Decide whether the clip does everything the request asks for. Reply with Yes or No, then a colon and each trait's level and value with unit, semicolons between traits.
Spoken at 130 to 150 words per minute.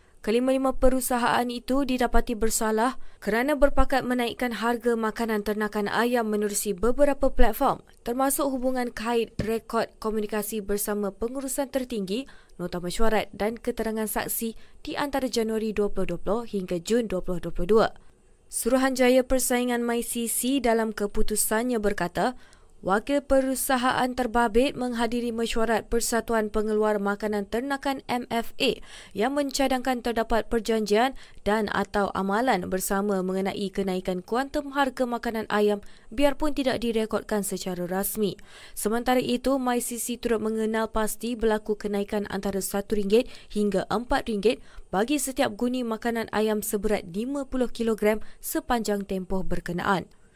No: average, 110 wpm